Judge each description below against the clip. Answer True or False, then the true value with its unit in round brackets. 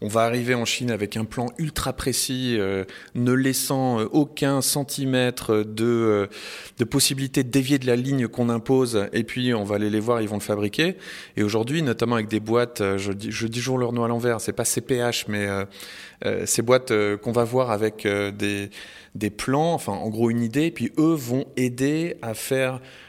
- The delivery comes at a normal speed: True (210 wpm)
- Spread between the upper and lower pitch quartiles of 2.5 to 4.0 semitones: True (3.3 semitones)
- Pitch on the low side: True (120 Hz)